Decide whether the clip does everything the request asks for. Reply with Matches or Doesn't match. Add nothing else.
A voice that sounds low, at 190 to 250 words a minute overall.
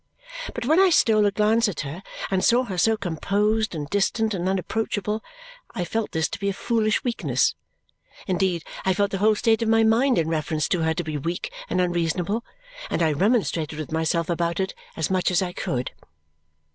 Doesn't match